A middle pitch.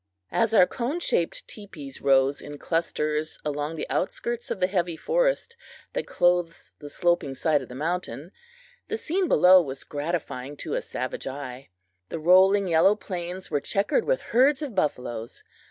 Yes: medium, 170 Hz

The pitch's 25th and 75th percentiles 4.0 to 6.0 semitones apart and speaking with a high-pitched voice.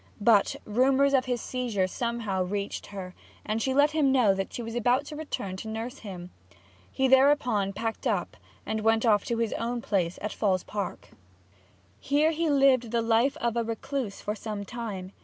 Yes: average, 4.3 semitones; high, 230 Hz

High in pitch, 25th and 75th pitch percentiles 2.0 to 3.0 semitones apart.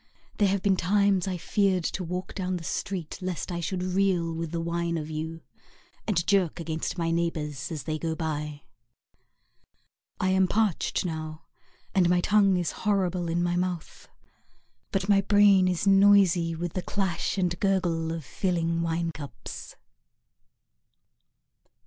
No: medium, 175 Hz; narrow, 2.5 semitones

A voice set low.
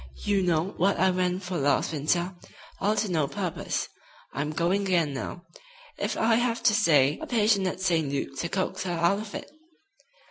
No: medium, 180 Hz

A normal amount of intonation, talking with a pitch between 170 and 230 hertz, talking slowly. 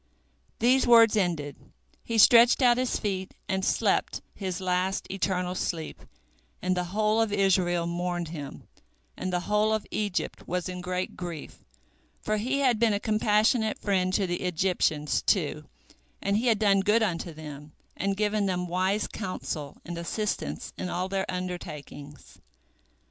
No: average, 3.3 semitones; medium, 185 Hz; average, 155 wpm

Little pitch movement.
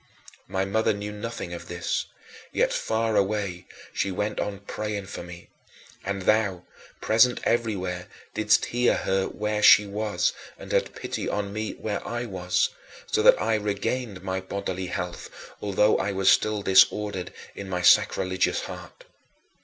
Yes: narrow, 2.3 semitones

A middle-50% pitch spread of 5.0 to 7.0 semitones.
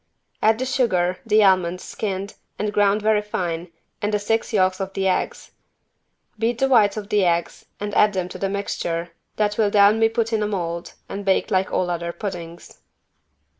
No: narrow, 2.6 semitones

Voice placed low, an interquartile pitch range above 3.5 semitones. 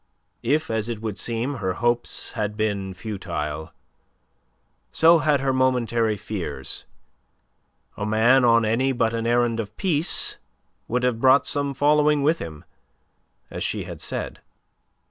Yes: low, 115 Hz; average, 3.9 semitones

